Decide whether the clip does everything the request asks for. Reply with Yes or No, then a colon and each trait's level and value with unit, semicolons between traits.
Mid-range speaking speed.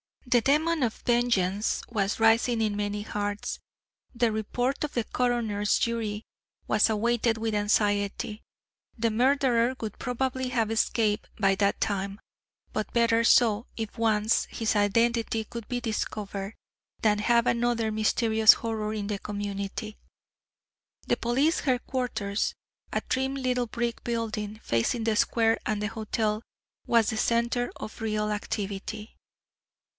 No: slow, 130 wpm